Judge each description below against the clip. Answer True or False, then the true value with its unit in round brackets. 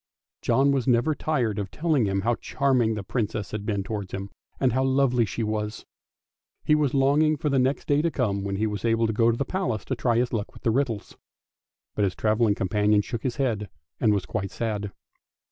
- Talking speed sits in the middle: False (215 wpm)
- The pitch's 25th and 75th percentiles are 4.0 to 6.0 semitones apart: True (4.4 semitones)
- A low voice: True (115 Hz)